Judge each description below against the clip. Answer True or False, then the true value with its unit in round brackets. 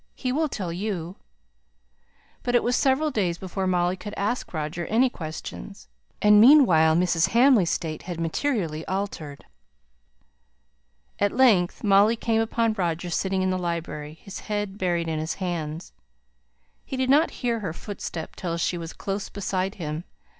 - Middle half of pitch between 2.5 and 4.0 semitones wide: False (4.8 semitones)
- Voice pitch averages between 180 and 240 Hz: True (190 Hz)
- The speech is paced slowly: False (155 wpm)